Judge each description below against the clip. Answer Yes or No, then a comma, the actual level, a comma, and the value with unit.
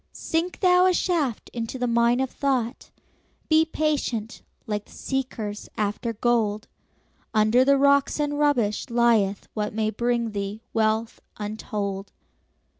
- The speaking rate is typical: No, slow, 130 wpm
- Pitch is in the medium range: No, high, 235 Hz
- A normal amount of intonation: Yes, average, 4.5 semitones